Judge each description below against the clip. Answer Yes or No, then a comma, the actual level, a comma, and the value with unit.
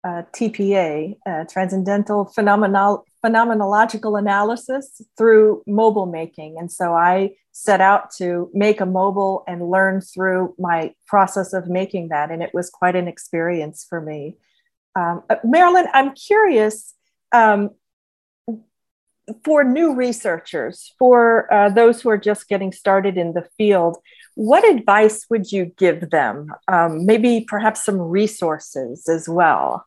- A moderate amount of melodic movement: Yes, average, 4.0 semitones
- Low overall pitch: No, high, 195 Hz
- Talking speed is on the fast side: No, slow, 135 wpm